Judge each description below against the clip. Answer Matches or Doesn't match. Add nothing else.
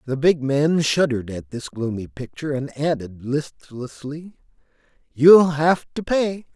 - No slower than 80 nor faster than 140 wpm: Matches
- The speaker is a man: Matches